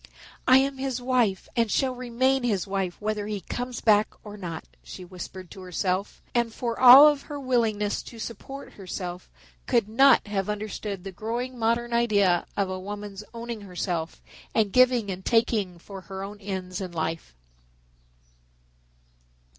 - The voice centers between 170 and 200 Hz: No, high, 210 Hz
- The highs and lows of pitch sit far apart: No, average, 4.1 semitones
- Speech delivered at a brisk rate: No, average, 155 wpm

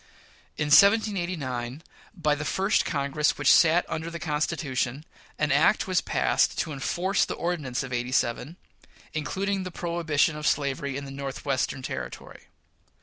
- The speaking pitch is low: No, medium, 150 Hz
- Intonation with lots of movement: No, average, 3.9 semitones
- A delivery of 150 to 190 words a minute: No, average, 140 wpm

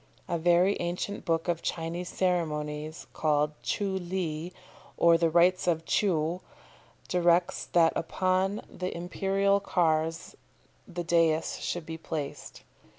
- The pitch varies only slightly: Yes, narrow, 2.0 semitones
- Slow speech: Yes, slow, 120 wpm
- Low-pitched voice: No, medium, 170 Hz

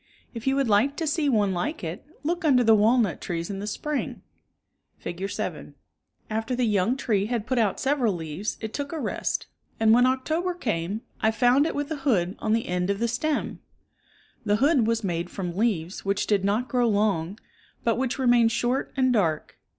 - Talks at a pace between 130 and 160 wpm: No, average, 195 wpm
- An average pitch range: Yes, average, 4.6 semitones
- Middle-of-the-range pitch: No, high, 225 Hz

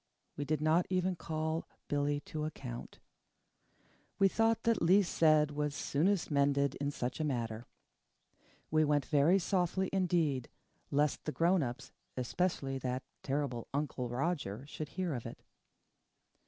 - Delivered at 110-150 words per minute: Yes, average, 140 wpm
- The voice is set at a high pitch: No, medium, 150 Hz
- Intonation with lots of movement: No, average, 3.7 semitones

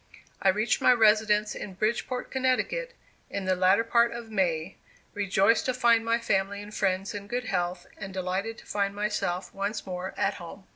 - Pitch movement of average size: Yes, average, 3.2 semitones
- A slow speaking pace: No, average, 180 wpm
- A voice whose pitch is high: Yes, high, 205 Hz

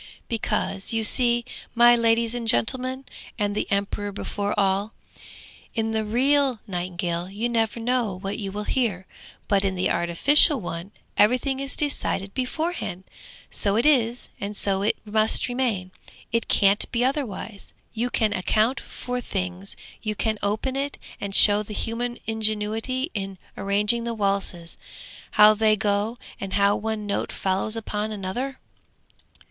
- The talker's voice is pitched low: No, high, 215 Hz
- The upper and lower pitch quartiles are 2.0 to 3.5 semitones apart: Yes, average, 3.2 semitones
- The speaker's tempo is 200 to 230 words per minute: No, average, 145 wpm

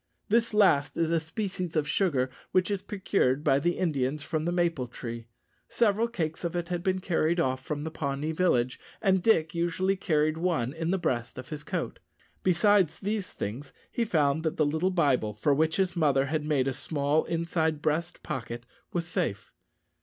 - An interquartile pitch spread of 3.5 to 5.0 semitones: Yes, average, 4.3 semitones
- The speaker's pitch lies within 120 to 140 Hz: No, medium, 160 Hz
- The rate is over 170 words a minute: Yes, average, 185 wpm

